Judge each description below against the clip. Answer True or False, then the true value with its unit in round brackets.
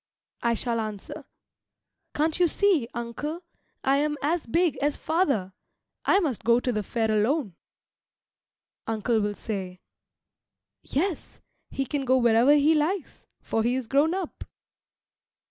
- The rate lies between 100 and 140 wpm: True (135 wpm)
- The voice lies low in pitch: False (265 Hz)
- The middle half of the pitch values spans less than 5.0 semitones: False (5.5 semitones)